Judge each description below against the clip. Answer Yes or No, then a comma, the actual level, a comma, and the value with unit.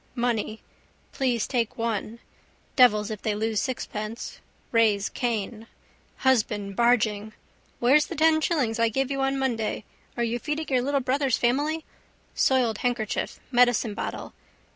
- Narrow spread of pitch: No, average, 3.4 semitones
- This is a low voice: No, high, 240 Hz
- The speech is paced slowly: Yes, slow, 130 wpm